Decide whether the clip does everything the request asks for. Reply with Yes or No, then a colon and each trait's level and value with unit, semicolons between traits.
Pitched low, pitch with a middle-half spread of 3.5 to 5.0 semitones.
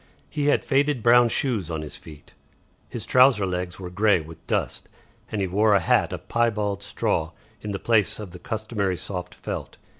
Yes: low, 105 Hz; average, 4.5 semitones